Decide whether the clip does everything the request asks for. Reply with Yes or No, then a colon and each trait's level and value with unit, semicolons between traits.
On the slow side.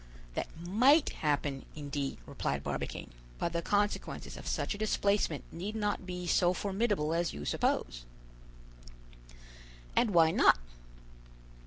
Yes: slow, 125 wpm